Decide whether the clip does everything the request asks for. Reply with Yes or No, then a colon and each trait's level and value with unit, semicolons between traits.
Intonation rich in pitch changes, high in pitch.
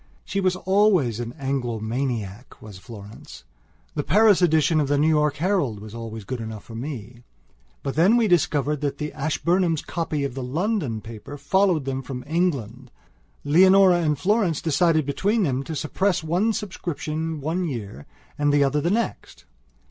No: wide, 6.1 semitones; medium, 150 Hz